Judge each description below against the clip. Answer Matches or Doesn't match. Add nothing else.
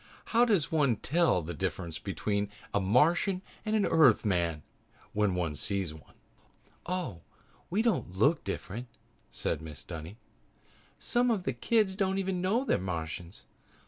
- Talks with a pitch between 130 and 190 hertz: Doesn't match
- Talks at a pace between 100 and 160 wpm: Matches